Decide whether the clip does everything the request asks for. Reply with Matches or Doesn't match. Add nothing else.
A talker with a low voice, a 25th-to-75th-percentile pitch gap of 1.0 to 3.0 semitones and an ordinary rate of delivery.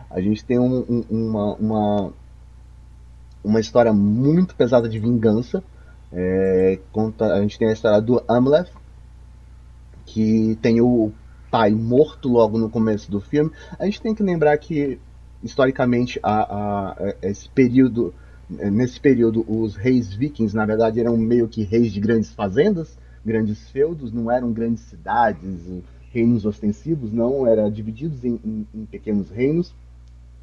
Doesn't match